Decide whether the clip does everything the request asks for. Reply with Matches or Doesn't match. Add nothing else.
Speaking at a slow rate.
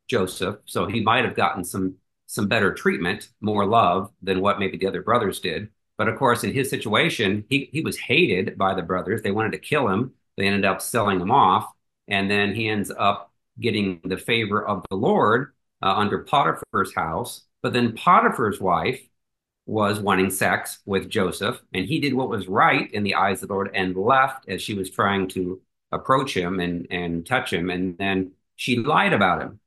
Doesn't match